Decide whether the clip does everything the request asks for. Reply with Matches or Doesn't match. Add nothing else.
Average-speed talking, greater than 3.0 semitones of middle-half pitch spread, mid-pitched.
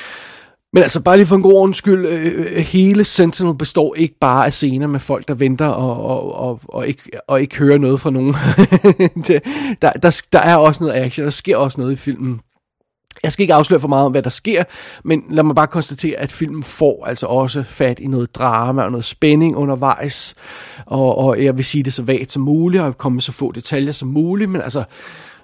Matches